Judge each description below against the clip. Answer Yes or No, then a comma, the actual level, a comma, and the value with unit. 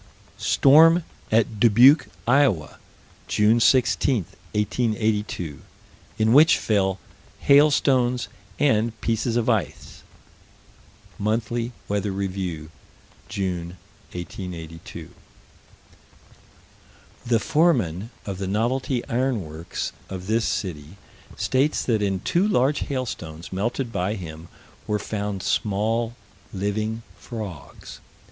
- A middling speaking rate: No, slow, 95 wpm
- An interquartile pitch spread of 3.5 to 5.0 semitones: Yes, average, 4.3 semitones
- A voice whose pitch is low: Yes, low, 110 Hz